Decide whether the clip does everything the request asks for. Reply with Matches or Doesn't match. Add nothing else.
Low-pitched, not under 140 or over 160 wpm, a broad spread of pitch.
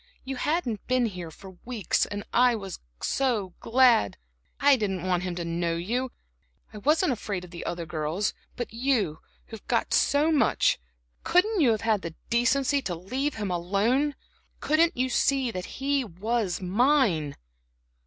Doesn't match